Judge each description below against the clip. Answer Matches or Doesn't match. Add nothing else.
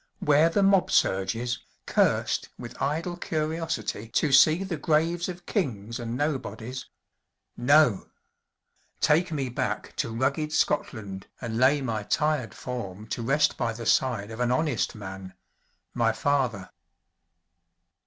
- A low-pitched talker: Matches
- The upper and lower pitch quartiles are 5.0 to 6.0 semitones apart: Matches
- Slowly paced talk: Matches